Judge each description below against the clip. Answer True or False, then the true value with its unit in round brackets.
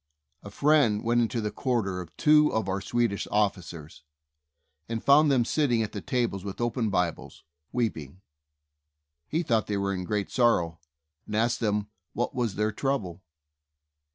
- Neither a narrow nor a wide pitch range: True (3.6 semitones)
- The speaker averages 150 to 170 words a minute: True (155 wpm)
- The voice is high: False (110 Hz)